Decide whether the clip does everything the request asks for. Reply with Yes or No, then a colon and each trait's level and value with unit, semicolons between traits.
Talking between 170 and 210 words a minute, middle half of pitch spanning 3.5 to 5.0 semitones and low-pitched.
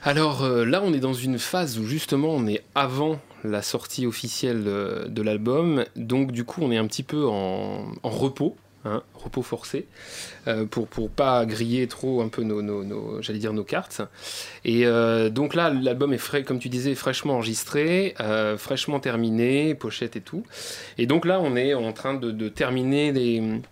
Yes: average, 195 wpm; average, 3.9 semitones; low, 125 Hz